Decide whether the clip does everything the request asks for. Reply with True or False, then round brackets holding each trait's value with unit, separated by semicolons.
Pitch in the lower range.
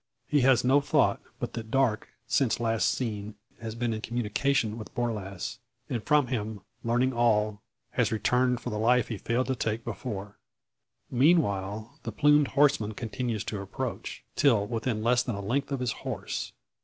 True (115 Hz)